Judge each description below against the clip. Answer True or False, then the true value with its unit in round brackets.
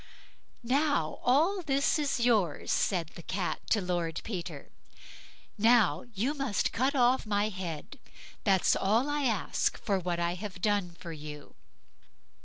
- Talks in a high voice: True (205 Hz)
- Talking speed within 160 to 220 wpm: False (140 wpm)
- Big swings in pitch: True (6.3 semitones)